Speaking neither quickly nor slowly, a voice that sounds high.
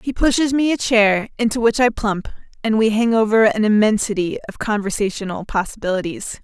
Yes: average, 170 wpm; high, 220 Hz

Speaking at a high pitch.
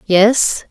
Yes: high, 210 Hz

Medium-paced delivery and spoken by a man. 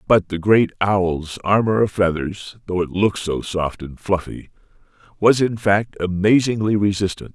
Yes: average, 155 wpm; male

